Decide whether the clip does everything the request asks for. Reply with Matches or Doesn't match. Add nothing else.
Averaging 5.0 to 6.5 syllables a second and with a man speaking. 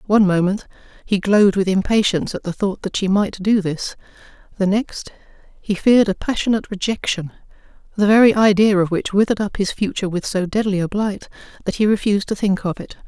Doesn't match